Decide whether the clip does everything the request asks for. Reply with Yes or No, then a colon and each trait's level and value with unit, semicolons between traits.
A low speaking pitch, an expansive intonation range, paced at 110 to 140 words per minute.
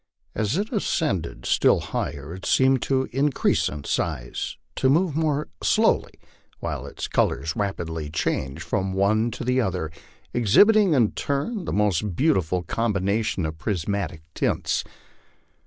Yes: low, 105 Hz; wide, 8.3 semitones; slow, 135 wpm